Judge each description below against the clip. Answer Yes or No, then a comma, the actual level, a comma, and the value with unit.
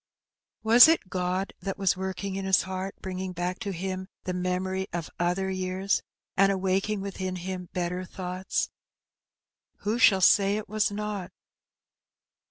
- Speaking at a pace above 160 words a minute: No, average, 145 wpm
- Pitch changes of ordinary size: No, narrow, 1.2 semitones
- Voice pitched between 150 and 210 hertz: Yes, high, 190 Hz